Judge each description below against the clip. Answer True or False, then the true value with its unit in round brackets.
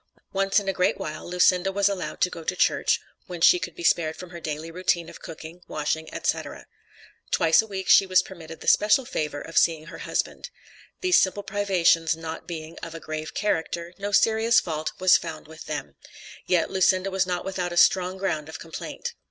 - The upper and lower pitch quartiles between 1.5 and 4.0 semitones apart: True (2.9 semitones)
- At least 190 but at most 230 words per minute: True (200 wpm)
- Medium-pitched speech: True (180 Hz)